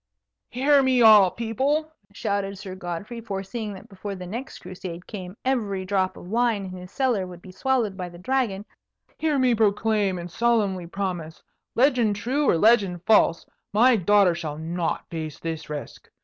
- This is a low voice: No, high, 200 Hz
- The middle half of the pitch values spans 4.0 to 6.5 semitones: Yes, average, 4.6 semitones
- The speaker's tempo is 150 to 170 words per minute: Yes, average, 165 wpm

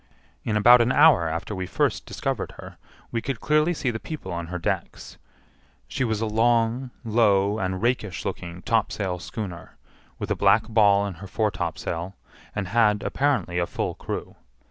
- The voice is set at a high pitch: No, low, 105 Hz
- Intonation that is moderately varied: Yes, average, 4.0 semitones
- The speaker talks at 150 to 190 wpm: Yes, average, 165 wpm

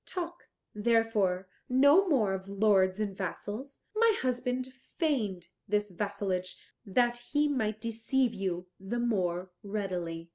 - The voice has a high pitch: Yes, high, 215 Hz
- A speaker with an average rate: No, slow, 120 wpm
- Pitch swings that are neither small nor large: Yes, average, 4.9 semitones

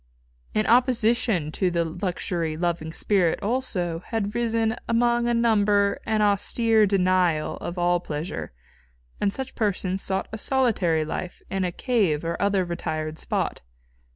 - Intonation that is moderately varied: Yes, average, 4.6 semitones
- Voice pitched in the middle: No, high, 195 Hz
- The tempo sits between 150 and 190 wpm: No, average, 140 wpm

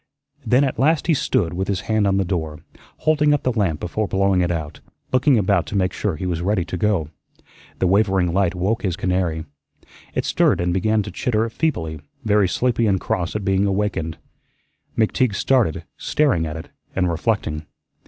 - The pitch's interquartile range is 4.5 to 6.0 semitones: No, average, 3.9 semitones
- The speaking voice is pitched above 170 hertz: No, very low, 95 Hz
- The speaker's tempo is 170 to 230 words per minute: Yes, average, 185 wpm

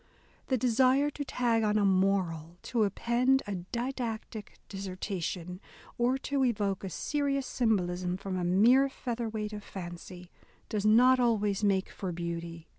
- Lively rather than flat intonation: No, average, 4.9 semitones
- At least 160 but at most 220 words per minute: No, average, 145 wpm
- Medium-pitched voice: No, high, 210 Hz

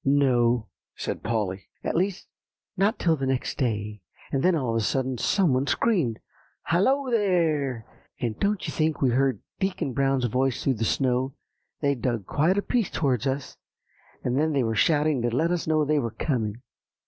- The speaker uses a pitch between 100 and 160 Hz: Yes, low, 135 Hz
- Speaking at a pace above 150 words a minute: Yes, average, 180 wpm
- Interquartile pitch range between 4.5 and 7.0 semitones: Yes, average, 5.1 semitones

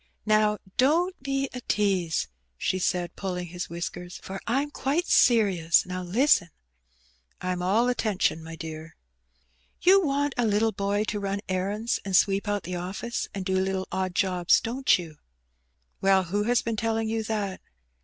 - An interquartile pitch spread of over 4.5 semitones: No, average, 4.0 semitones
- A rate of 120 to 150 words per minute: No, average, 165 wpm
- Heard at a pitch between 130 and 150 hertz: No, high, 195 Hz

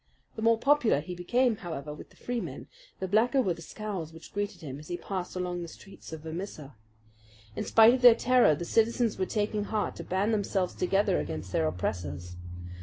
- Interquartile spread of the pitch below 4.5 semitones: No, wide, 5.6 semitones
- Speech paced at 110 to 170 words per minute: No, average, 195 wpm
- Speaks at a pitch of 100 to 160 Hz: No, high, 190 Hz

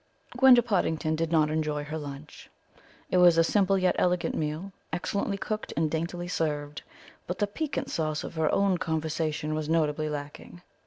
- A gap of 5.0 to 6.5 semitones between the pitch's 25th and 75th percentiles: No, average, 3.1 semitones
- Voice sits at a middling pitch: Yes, medium, 160 Hz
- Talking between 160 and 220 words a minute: Yes, average, 165 wpm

